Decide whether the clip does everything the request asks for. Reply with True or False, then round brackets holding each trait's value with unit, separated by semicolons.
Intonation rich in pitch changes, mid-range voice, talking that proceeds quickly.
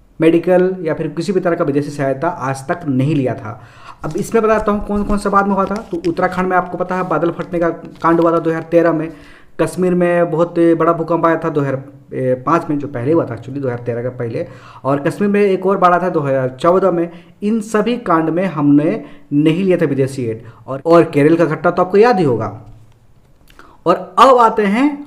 False (4.4 semitones; 165 Hz; 225 wpm)